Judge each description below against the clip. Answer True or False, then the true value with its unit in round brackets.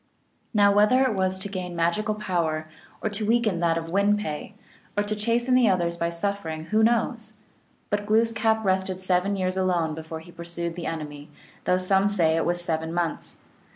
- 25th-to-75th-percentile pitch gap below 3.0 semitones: False (3.8 semitones)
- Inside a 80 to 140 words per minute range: False (185 wpm)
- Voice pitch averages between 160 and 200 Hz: True (185 Hz)